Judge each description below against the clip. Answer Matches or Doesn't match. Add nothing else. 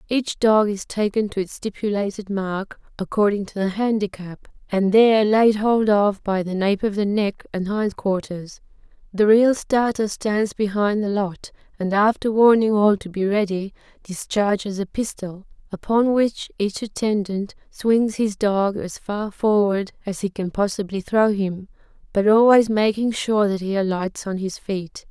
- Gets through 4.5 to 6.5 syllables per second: Doesn't match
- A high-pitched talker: Matches